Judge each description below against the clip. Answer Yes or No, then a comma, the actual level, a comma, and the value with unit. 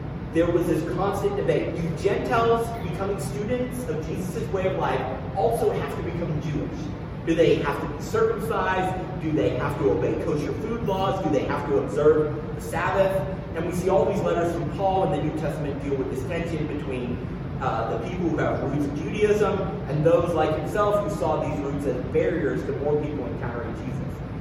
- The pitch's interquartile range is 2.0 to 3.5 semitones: Yes, average, 3.2 semitones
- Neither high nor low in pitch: Yes, medium, 155 Hz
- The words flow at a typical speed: Yes, average, 195 wpm